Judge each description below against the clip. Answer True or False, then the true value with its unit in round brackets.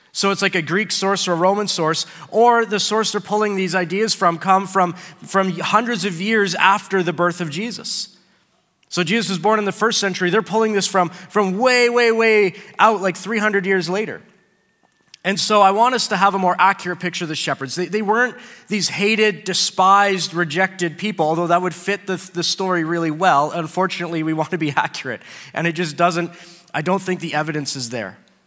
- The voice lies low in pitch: False (190 Hz)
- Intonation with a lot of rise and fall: False (2.9 semitones)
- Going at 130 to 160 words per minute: False (205 wpm)